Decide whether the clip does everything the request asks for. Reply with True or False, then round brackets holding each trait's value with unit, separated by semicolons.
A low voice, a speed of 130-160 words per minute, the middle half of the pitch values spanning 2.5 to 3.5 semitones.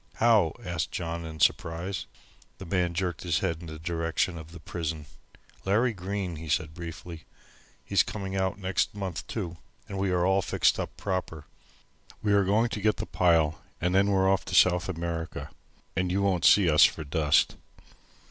False (90 Hz; 180 wpm; 2.8 semitones)